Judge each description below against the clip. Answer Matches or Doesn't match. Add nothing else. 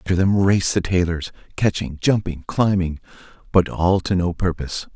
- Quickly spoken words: Doesn't match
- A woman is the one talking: Doesn't match